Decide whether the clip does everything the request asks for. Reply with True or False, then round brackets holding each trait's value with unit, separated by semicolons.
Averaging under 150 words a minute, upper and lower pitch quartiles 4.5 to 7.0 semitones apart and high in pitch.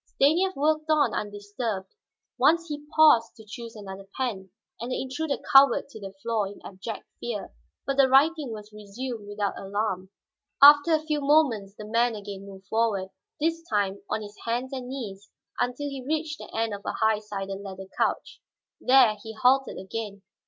False (175 wpm; 5.2 semitones; 230 Hz)